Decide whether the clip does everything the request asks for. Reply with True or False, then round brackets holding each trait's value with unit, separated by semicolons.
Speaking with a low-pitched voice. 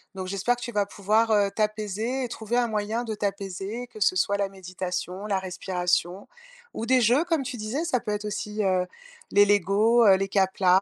False (205 Hz)